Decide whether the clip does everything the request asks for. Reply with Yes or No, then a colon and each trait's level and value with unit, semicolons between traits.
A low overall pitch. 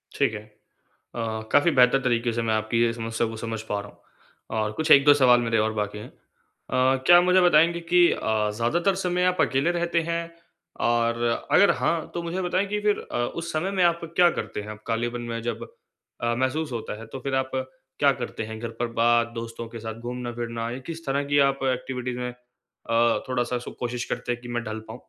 Yes: low, 125 Hz